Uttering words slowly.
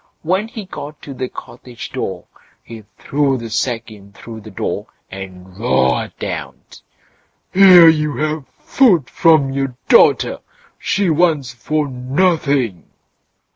Yes: slow, 130 wpm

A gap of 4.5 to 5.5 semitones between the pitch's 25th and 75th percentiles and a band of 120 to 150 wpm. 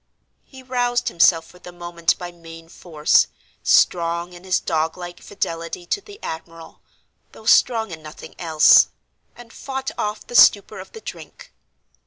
Yes: average, 5.0 semitones; average, 145 wpm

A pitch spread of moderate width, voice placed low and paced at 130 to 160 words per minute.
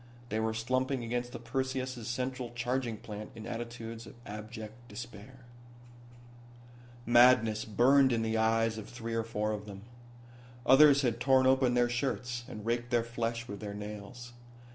No: narrow, 2.1 semitones; low, 120 Hz; average, 155 wpm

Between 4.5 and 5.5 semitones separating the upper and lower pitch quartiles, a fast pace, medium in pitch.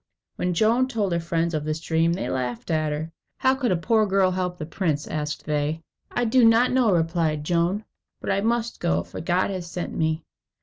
Yes: average, 5.0 semitones; fast, 210 wpm; medium, 170 Hz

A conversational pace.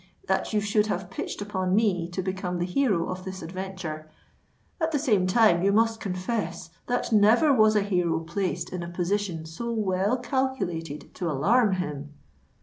Yes: average, 170 wpm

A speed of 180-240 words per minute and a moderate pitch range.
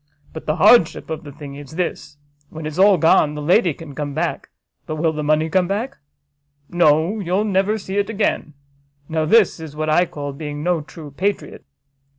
Yes: average, 190 wpm; average, 4.0 semitones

